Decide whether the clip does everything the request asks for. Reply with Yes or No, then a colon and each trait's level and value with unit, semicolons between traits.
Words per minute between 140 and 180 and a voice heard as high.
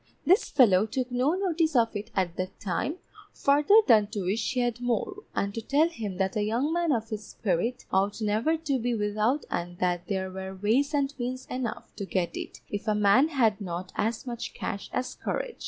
No: fast, 205 wpm; high, 225 Hz